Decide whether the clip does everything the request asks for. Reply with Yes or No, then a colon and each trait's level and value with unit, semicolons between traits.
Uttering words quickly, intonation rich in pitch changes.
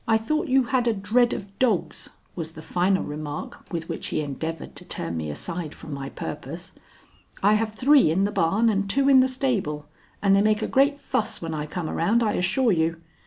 Yes: fast, 215 wpm; wide, 6.5 semitones